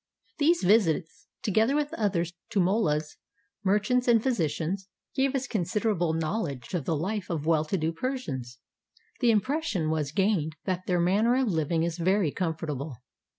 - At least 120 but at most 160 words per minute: Yes, average, 155 wpm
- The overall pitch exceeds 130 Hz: Yes, medium, 185 Hz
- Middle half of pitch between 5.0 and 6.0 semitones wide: Yes, wide, 5.5 semitones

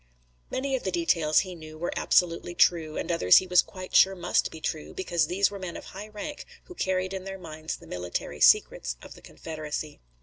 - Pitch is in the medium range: Yes, medium, 175 Hz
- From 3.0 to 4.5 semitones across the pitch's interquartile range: Yes, average, 3.4 semitones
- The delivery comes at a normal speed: No, fast, 210 wpm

